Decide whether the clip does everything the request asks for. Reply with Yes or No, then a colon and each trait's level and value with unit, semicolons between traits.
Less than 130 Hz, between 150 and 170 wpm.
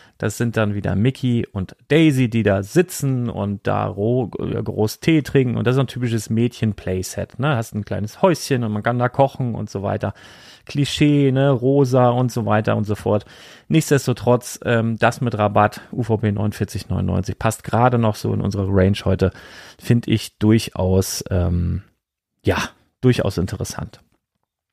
Yes: low, 115 Hz; average, 160 wpm